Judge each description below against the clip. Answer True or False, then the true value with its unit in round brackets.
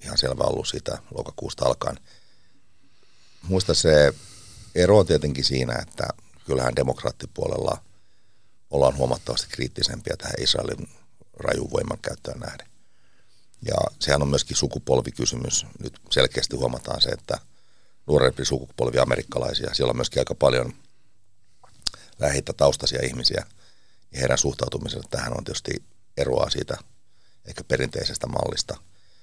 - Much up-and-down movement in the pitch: True (6.0 semitones)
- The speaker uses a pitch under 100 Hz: True (70 Hz)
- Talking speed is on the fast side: False (115 wpm)